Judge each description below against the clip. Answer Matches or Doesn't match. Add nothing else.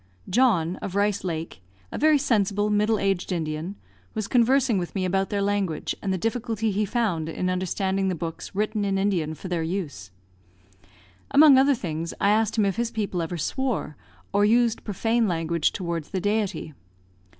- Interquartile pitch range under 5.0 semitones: Matches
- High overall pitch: Matches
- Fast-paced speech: Doesn't match